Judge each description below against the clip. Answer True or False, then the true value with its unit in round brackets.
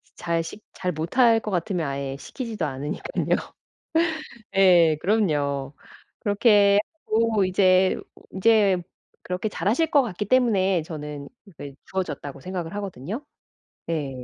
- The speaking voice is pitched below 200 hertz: True (185 Hz)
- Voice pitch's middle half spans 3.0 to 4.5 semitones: False (5.3 semitones)